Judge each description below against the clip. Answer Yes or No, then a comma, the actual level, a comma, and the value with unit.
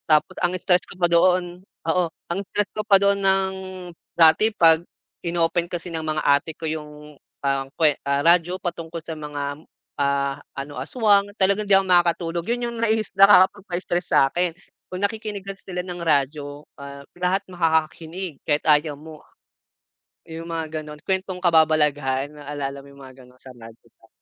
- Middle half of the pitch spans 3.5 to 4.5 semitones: Yes, average, 3.8 semitones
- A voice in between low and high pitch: Yes, medium, 165 Hz